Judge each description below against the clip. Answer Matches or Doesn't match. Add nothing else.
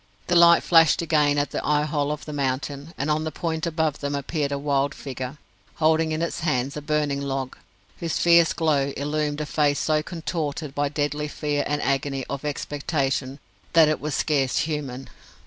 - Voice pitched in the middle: Matches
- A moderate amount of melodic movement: Doesn't match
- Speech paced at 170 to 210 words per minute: Matches